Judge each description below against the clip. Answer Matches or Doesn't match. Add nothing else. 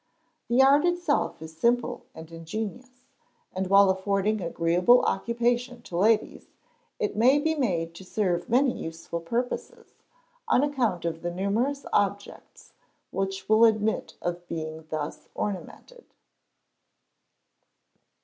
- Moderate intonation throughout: Doesn't match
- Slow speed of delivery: Matches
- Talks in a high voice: Matches